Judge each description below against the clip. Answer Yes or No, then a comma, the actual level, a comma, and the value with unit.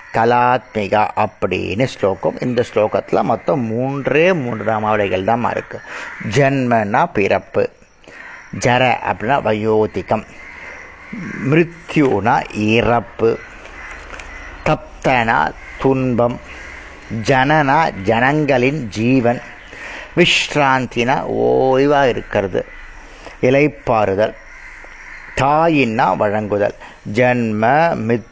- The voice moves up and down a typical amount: Yes, average, 3.9 semitones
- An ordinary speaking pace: No, slow, 65 wpm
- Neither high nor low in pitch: No, low, 120 Hz